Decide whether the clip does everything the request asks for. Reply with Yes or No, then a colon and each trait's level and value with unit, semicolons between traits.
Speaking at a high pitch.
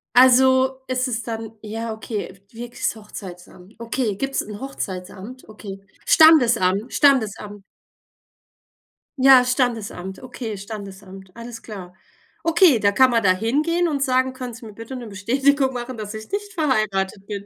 Yes: high, 230 Hz